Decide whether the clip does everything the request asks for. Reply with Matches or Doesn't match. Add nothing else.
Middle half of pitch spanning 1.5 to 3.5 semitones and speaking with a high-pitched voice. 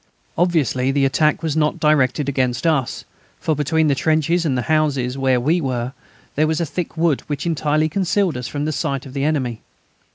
Doesn't match